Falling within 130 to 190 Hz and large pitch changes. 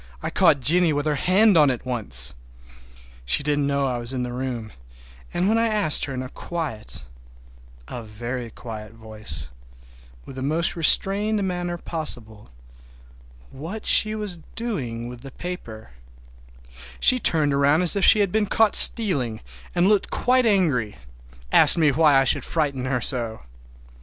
Yes: medium, 140 Hz; wide, 7.2 semitones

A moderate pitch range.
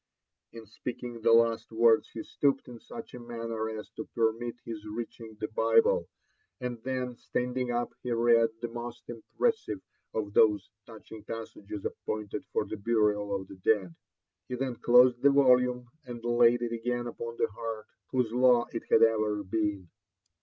No: narrow, 1.9 semitones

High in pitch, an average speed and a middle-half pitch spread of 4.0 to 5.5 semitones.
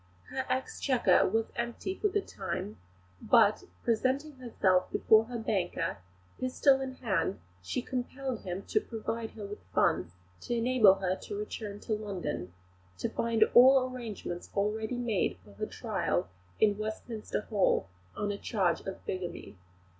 Yes: high, 220 Hz; average, 145 wpm; average, 4.5 semitones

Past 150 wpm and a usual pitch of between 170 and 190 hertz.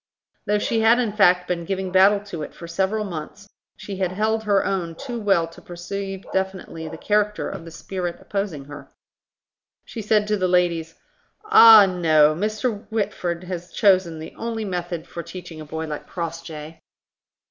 Yes: average, 170 wpm; medium, 185 Hz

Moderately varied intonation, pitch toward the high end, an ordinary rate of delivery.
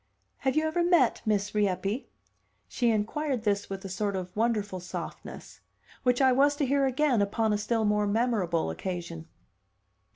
Yes: average, 4.7 semitones; high, 215 Hz; average, 160 wpm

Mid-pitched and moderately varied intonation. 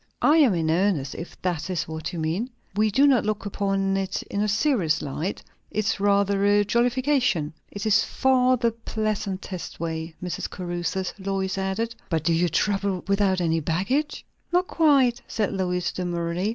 No: high, 195 Hz; average, 3.8 semitones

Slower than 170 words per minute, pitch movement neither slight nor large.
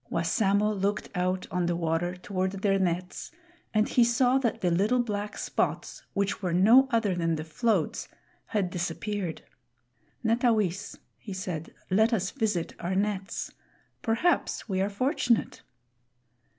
Yes: slow, 135 wpm; average, 3.6 semitones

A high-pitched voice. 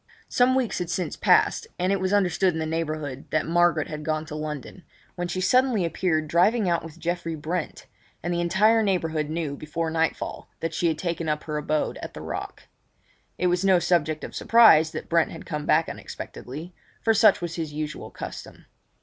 No: medium, 165 Hz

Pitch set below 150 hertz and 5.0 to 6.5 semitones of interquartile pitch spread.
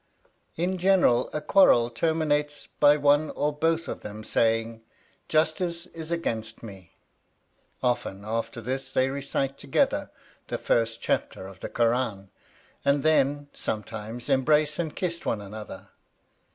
Yes: low, 135 Hz; wide, 5.5 semitones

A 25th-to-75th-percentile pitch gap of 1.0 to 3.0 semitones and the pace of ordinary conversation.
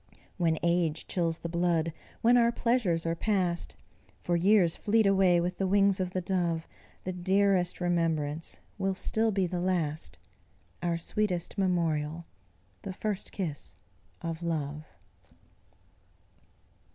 No: average, 2.7 semitones; slow, 125 wpm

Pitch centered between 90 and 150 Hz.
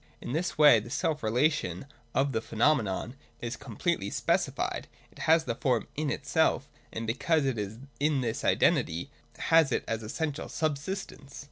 Yes: low, 135 Hz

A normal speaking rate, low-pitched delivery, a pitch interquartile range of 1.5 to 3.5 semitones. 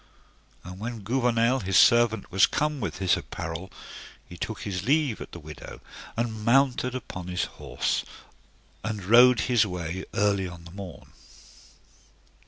No: average, 145 wpm; low, 105 Hz; average, 4.7 semitones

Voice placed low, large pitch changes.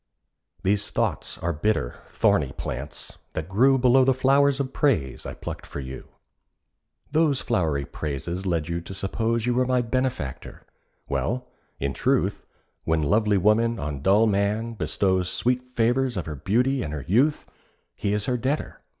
Yes: low, 105 Hz; wide, 7.0 semitones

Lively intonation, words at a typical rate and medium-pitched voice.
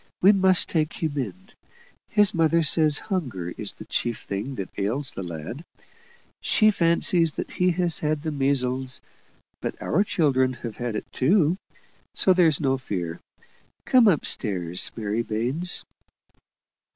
Yes: wide, 6.5 semitones; average, 145 wpm; medium, 145 Hz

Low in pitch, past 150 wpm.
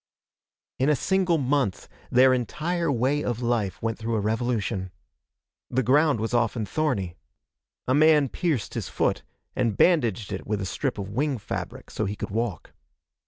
Yes: low, 120 Hz; average, 165 wpm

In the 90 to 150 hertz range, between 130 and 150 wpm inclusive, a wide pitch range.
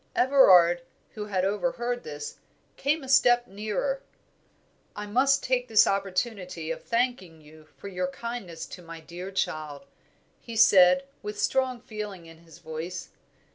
No: high, 200 Hz; average, 140 wpm; wide, 6.0 semitones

